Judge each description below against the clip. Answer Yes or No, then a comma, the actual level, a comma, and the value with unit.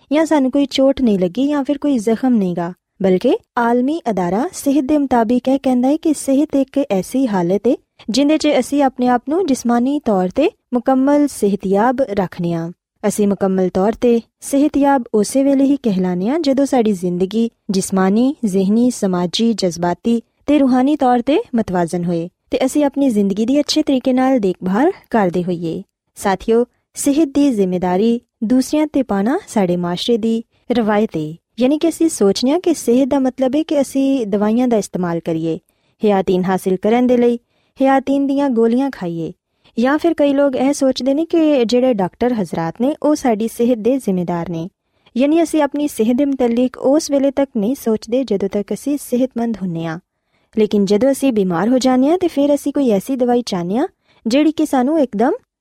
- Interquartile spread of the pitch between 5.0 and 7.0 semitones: Yes, wide, 5.6 semitones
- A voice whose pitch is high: Yes, high, 245 Hz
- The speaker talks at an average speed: Yes, average, 180 wpm